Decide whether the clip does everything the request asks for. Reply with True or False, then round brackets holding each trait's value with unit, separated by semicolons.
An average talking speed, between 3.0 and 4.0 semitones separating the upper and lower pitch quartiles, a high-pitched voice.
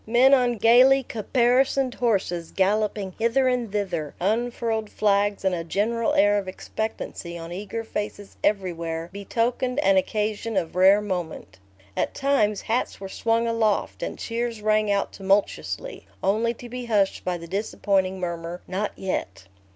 True (145 wpm; 3.5 semitones; 210 Hz)